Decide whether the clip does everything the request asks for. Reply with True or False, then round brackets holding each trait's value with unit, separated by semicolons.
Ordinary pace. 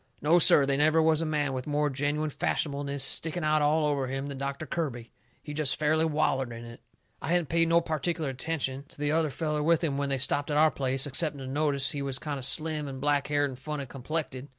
False (230 wpm)